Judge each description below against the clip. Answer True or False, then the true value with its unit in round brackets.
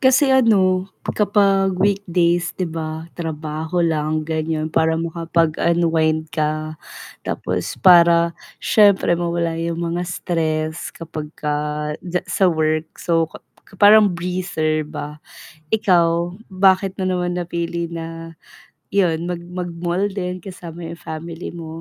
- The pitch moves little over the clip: True (2.2 semitones)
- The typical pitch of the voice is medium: True (170 Hz)